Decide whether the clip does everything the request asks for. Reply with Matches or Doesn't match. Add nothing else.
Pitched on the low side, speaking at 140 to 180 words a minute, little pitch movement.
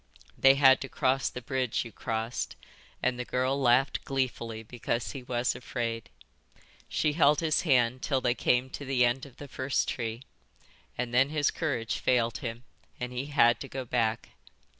Matches